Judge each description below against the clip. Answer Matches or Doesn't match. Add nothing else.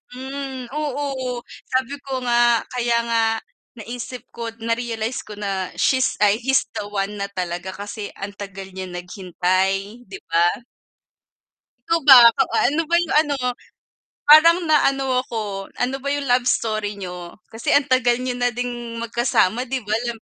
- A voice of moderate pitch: Doesn't match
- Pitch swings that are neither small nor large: Matches